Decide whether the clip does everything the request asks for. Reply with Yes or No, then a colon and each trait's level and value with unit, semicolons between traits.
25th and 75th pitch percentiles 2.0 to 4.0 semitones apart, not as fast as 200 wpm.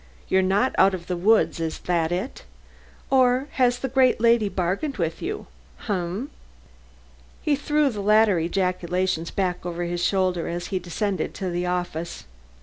No: average, 5.0 semitones; average, 160 wpm